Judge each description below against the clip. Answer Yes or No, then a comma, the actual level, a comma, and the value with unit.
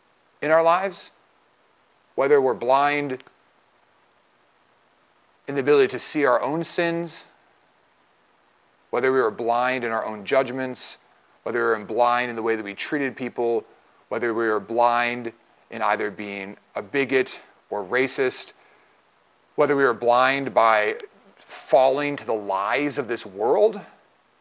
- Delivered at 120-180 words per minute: Yes, average, 140 wpm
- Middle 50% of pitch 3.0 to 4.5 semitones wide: No, average, 4.9 semitones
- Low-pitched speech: Yes, low, 130 Hz